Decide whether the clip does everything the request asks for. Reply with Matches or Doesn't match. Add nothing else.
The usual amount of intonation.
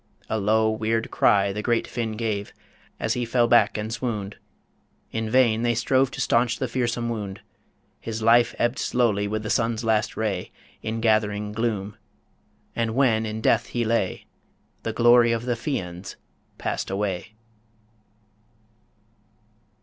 Doesn't match